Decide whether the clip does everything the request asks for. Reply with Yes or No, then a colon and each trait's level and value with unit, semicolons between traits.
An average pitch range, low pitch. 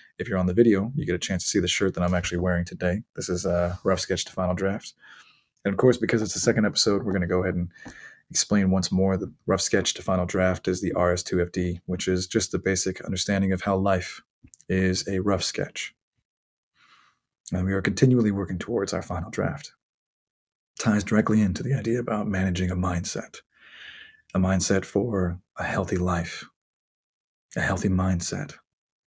No: narrow, 1.7 semitones; very low, 95 Hz